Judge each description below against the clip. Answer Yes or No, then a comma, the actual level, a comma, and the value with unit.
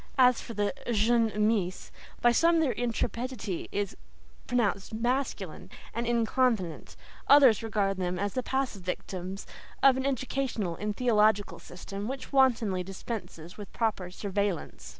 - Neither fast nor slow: No, slow, 130 wpm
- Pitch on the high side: Yes, high, 220 Hz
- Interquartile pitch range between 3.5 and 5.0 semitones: Yes, average, 4.0 semitones